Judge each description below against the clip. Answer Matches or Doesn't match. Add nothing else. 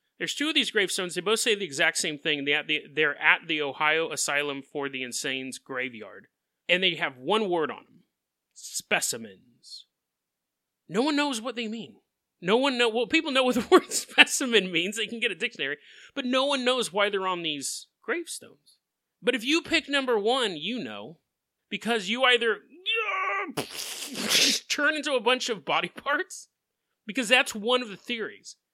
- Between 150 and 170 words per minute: Doesn't match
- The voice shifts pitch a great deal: Matches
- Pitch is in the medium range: Doesn't match